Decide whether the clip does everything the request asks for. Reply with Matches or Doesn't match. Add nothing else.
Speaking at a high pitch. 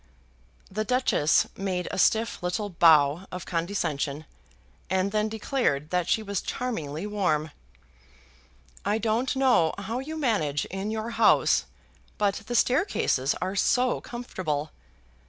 Matches